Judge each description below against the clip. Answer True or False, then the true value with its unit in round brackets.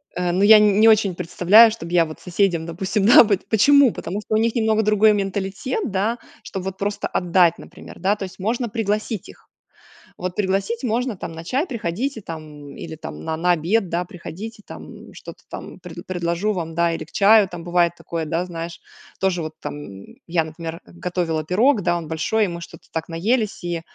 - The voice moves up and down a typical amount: True (4.1 semitones)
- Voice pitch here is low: False (185 Hz)